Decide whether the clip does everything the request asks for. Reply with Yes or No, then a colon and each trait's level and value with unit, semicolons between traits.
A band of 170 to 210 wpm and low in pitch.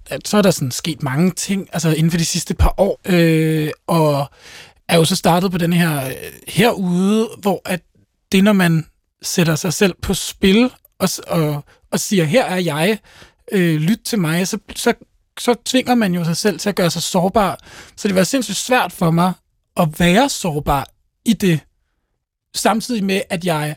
No: average, 190 wpm; medium, 180 Hz